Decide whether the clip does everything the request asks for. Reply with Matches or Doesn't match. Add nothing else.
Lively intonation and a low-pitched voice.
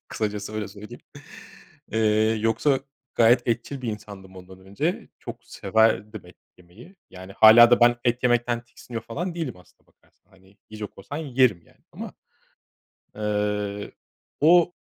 Doesn't match